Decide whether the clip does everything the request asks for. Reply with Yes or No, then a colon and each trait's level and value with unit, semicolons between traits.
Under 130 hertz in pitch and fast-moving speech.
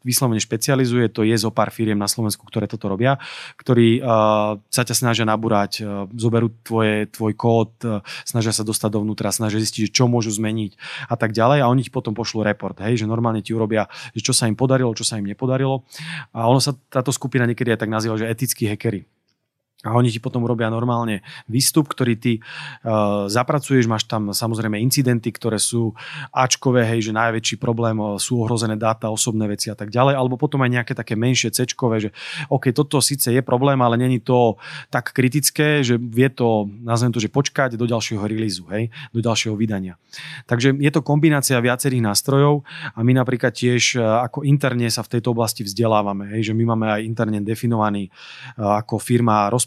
Yes: low, 115 Hz; fast, 190 wpm